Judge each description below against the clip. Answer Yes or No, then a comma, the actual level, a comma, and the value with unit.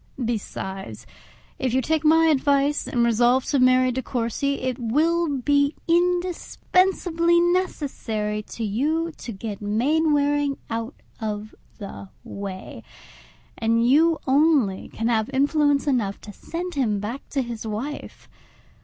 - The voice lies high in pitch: Yes, very high, 260 Hz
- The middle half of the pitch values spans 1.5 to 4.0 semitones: No, wide, 5.4 semitones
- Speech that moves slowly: Yes, slow, 125 wpm